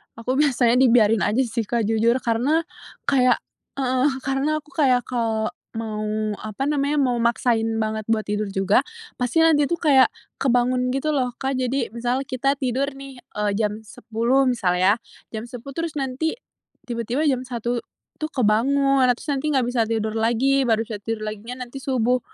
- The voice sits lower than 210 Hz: No, very high, 250 Hz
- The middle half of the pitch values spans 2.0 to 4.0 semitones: Yes, average, 3.3 semitones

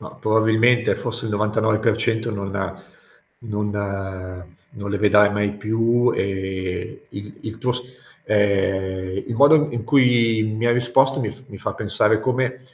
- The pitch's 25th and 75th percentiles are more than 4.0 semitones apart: No, narrow, 2.6 semitones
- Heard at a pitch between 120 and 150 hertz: No, low, 110 Hz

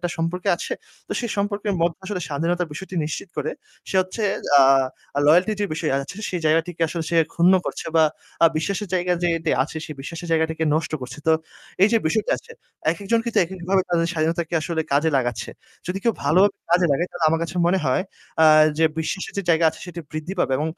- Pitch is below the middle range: No, medium, 170 Hz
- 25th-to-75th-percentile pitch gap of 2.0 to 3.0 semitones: Yes, average, 2.7 semitones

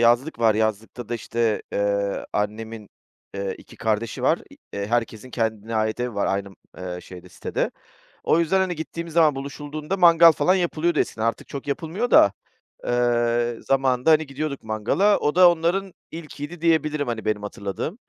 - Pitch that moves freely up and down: Yes, wide, 6.7 semitones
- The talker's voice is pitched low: Yes, low, 120 Hz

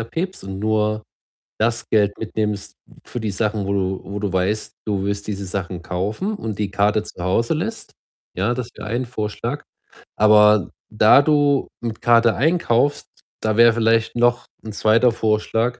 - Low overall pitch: Yes, low, 110 Hz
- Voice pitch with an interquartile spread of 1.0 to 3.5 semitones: Yes, average, 2.7 semitones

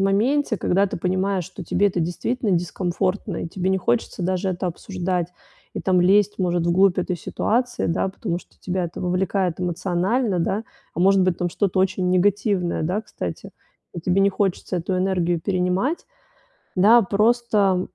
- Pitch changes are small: Yes, narrow, 2.0 semitones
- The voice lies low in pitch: No, medium, 185 Hz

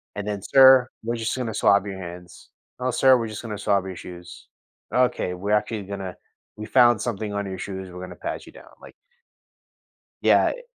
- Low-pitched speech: Yes, low, 105 Hz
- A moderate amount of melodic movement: Yes, average, 3.9 semitones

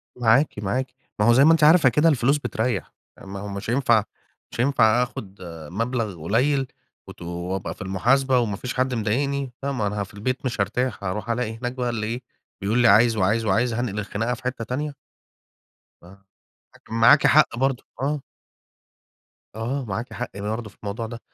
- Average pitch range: Yes, average, 3.7 semitones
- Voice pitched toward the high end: No, low, 115 Hz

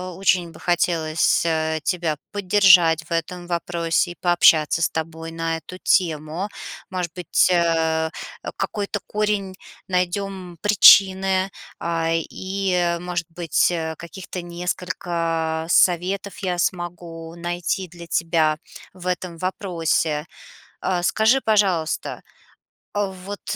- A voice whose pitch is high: No, medium, 175 Hz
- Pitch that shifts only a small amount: Yes, narrow, 2.2 semitones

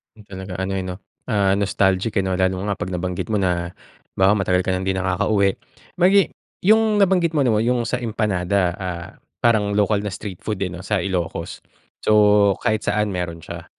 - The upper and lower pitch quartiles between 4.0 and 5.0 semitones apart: No, average, 2.7 semitones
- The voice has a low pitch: Yes, low, 100 Hz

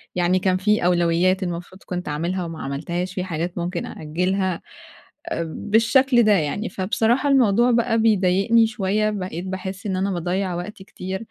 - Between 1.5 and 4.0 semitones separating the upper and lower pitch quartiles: Yes, average, 3.2 semitones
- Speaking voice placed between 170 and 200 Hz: Yes, high, 190 Hz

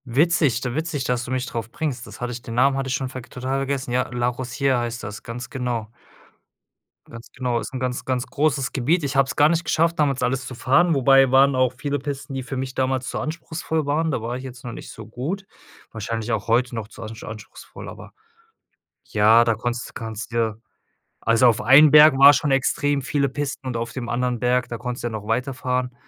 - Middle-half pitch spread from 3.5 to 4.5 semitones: No, average, 2.7 semitones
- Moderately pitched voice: No, low, 130 Hz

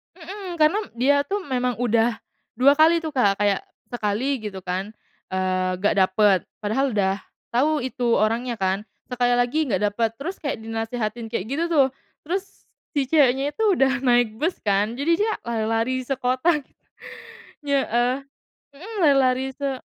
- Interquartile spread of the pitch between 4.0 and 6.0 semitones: Yes, average, 4.5 semitones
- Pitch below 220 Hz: No, very high, 250 Hz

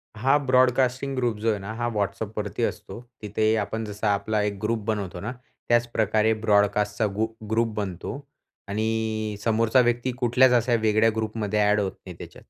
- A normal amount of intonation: No, narrow, 2.2 semitones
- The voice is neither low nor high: No, low, 110 Hz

